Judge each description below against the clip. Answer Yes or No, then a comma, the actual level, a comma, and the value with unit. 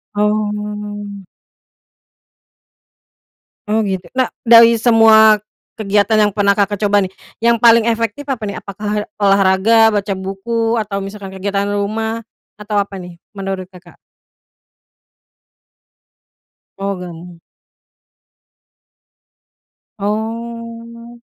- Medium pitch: No, high, 210 Hz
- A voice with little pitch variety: Yes, narrow, 2.3 semitones